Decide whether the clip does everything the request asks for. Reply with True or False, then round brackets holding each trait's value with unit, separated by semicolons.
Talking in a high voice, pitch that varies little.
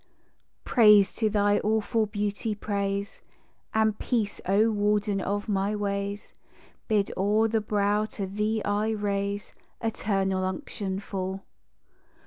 True (205 Hz; 1.3 semitones)